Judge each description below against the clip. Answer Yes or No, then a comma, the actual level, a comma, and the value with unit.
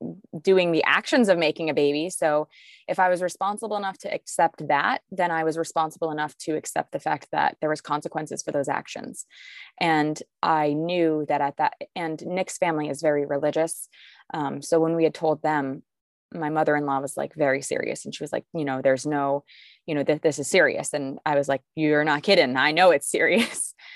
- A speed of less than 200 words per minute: No, fast, 205 wpm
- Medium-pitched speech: Yes, medium, 155 Hz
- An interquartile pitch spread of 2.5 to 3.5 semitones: Yes, average, 3.1 semitones